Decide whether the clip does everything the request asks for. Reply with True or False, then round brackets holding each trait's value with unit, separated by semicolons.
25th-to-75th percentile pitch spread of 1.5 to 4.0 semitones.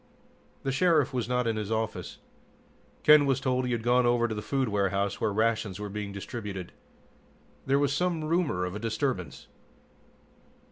False (4.6 semitones)